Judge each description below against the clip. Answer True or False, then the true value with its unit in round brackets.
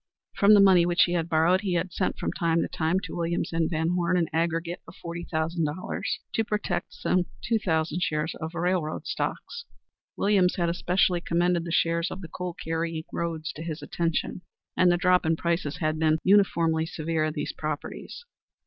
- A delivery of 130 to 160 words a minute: False (195 wpm)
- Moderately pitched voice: True (170 Hz)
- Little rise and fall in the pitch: True (1.9 semitones)